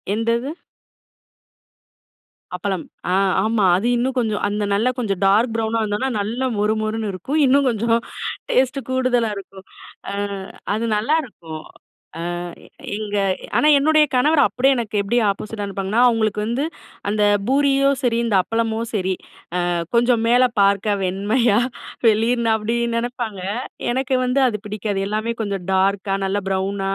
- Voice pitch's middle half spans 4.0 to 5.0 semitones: No, average, 3.4 semitones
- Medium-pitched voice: No, high, 220 Hz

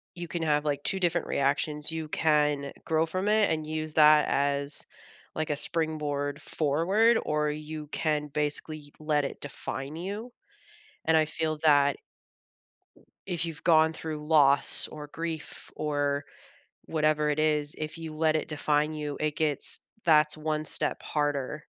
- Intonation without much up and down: Yes, narrow, 1.3 semitones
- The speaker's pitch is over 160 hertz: No, medium, 155 Hz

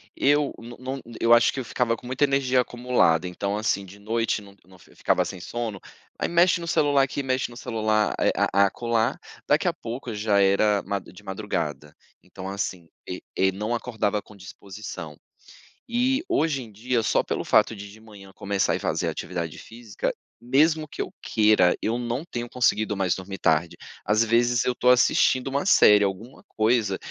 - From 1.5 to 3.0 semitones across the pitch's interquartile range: No, average, 4.1 semitones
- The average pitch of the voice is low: Yes, low, 110 Hz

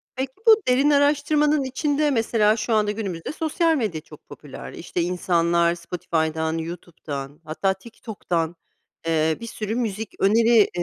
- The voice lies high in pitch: Yes, high, 210 Hz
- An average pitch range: No, wide, 7.6 semitones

